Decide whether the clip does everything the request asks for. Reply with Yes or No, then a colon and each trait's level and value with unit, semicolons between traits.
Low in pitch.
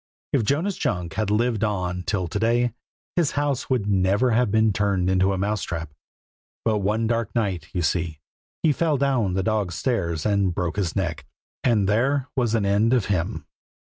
Yes: low, 105 Hz